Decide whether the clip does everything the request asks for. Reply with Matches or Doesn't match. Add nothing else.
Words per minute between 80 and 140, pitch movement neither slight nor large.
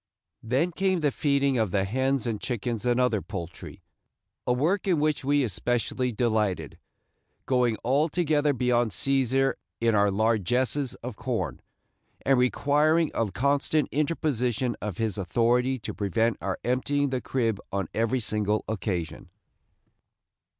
Matches